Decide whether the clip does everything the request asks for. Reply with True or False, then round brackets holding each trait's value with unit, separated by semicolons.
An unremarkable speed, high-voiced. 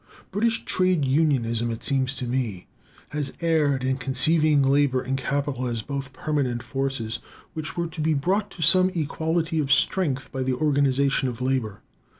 False (160 wpm; 140 Hz)